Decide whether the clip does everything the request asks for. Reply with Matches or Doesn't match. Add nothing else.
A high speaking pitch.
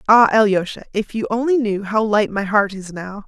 Matches